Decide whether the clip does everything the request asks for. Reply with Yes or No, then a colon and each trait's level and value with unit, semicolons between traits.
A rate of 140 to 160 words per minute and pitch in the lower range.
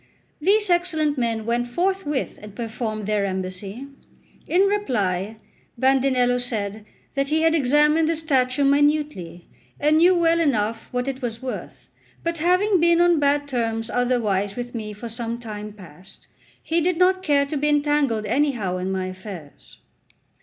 No: average, 155 wpm; very high, 255 Hz